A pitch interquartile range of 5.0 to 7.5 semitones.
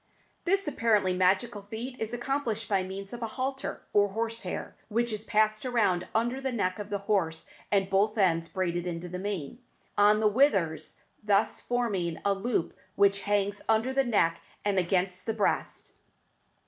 No: average, 3.4 semitones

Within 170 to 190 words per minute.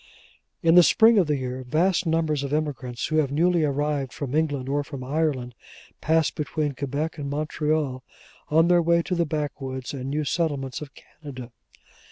Yes: average, 175 wpm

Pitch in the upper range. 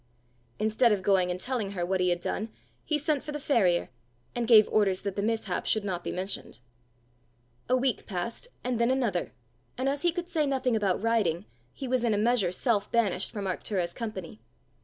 Yes: high, 215 Hz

